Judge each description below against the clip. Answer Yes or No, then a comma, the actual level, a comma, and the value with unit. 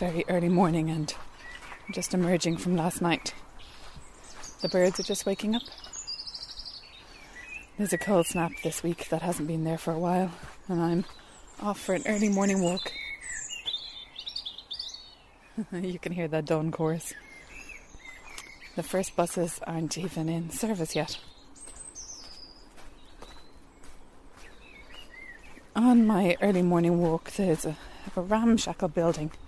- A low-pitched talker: No, medium, 175 Hz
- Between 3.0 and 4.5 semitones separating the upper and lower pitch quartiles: No, narrow, 2.5 semitones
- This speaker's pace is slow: Yes, slow, 120 wpm